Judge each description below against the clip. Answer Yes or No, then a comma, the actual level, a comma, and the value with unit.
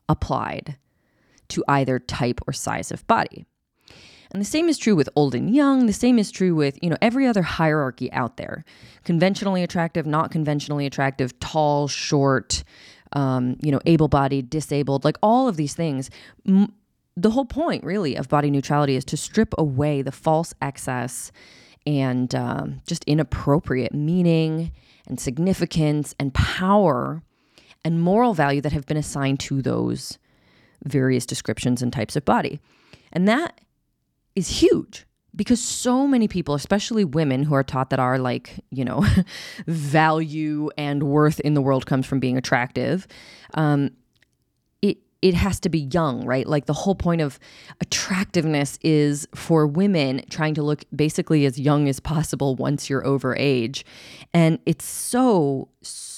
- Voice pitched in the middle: Yes, medium, 150 Hz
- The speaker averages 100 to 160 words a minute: Yes, average, 155 wpm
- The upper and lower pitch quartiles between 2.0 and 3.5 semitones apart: No, average, 4.1 semitones